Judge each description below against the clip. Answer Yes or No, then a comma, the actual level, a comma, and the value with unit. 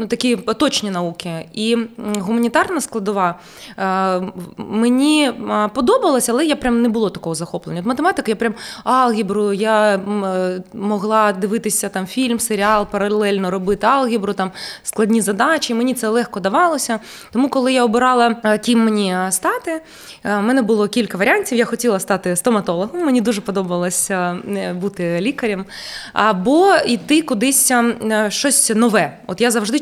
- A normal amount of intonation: Yes, average, 3.5 semitones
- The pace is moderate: Yes, average, 130 wpm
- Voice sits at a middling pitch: No, high, 220 Hz